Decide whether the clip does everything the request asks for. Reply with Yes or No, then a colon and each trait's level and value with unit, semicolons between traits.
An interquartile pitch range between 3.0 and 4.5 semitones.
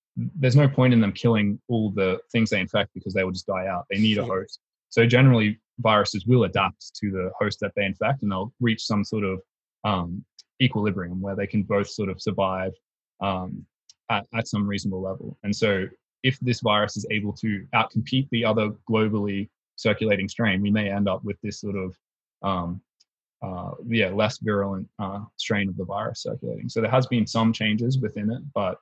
No: narrow, 2.4 semitones